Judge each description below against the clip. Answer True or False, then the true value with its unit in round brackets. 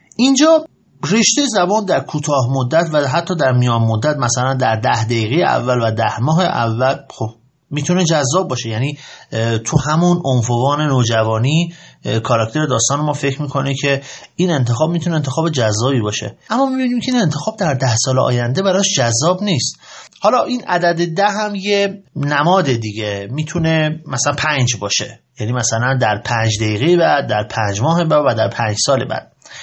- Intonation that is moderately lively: False (6.3 semitones)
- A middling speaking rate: False (160 wpm)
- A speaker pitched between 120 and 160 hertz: True (140 Hz)